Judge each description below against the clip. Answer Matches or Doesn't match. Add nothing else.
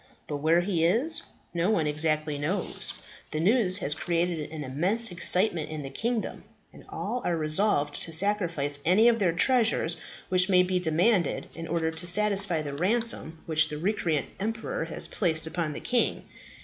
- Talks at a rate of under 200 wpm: Matches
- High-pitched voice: Doesn't match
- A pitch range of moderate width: Matches